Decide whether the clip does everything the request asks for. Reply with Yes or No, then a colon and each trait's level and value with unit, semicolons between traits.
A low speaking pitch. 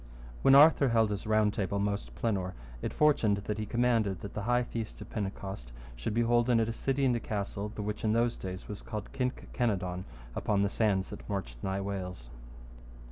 Yes: low, 105 Hz